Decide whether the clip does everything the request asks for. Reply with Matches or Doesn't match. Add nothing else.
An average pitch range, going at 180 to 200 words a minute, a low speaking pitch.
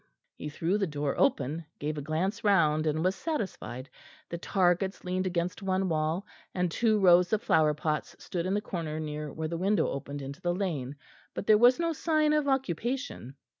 Doesn't match